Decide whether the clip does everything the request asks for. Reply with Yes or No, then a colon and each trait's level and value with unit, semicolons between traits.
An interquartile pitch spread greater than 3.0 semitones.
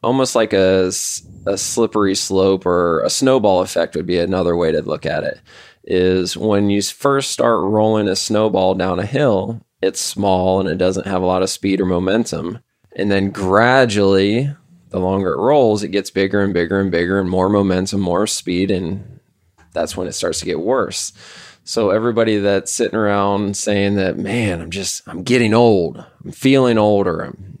No: narrow, 2.6 semitones